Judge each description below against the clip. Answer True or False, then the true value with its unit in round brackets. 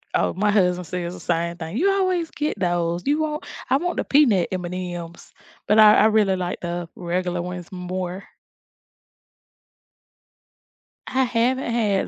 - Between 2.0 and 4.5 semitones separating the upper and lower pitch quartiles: False (5.3 semitones)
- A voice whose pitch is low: False (185 Hz)